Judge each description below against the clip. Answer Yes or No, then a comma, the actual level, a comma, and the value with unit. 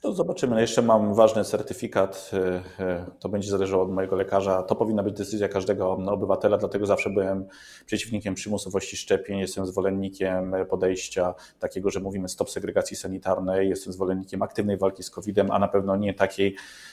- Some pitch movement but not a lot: No, narrow, 1.2 semitones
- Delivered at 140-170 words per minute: Yes, average, 155 wpm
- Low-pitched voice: Yes, very low, 95 Hz